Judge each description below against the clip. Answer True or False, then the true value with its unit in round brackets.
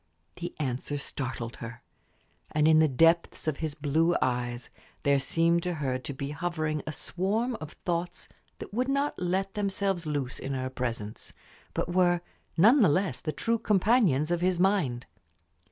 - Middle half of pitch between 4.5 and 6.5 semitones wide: True (5.2 semitones)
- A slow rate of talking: False (165 wpm)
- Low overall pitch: False (160 Hz)